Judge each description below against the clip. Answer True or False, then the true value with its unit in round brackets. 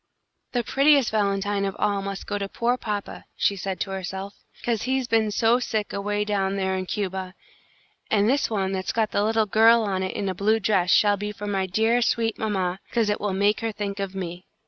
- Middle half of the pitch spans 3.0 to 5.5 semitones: False (2.4 semitones)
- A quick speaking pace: True (215 wpm)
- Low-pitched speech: False (205 Hz)